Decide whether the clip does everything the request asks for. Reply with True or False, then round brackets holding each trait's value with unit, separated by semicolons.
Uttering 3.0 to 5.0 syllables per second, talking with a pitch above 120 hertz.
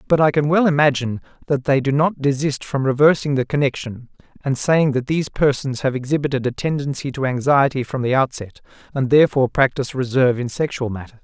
False (6.1 syllables/s; 135 Hz)